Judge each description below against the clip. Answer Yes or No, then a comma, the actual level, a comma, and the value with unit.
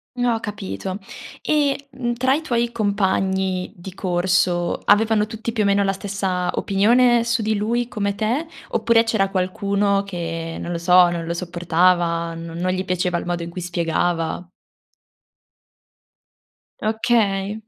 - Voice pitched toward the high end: Yes, high, 195 Hz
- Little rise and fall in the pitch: No, average, 4.1 semitones